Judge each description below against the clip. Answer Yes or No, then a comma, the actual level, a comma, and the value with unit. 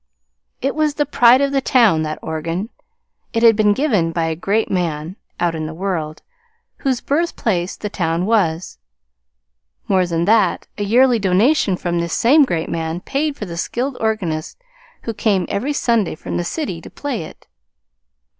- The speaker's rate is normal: Yes, average, 170 wpm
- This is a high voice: Yes, high, 200 Hz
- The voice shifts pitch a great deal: Yes, wide, 6.3 semitones